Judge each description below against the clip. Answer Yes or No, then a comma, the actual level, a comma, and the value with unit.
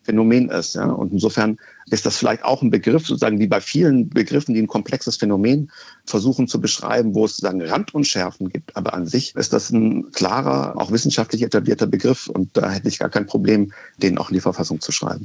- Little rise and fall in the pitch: No, average, 4.1 semitones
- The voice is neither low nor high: No, low, 110 Hz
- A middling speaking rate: No, fast, 210 wpm